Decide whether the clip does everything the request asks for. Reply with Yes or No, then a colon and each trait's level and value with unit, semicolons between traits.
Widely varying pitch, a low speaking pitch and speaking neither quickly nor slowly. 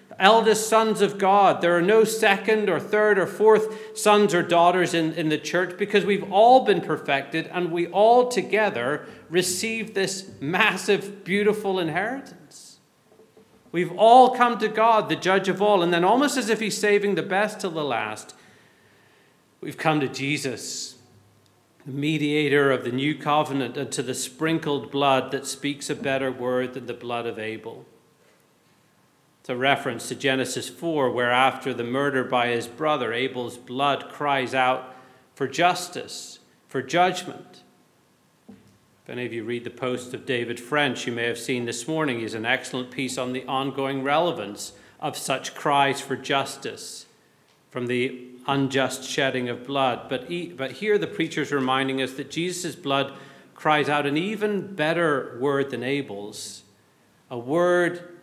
No: wide, 5.9 semitones; medium, 145 Hz; average, 160 wpm